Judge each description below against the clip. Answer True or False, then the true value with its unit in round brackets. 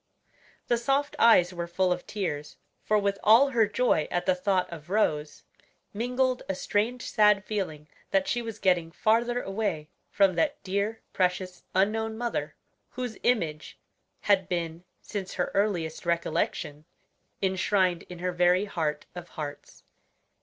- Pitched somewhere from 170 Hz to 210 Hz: True (190 Hz)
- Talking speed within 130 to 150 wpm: True (145 wpm)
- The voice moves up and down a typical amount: True (4.0 semitones)